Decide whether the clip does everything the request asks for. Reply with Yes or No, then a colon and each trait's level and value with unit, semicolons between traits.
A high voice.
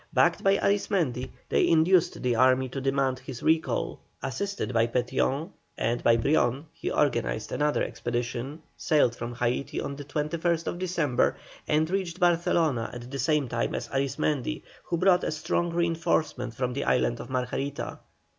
No: medium, 140 Hz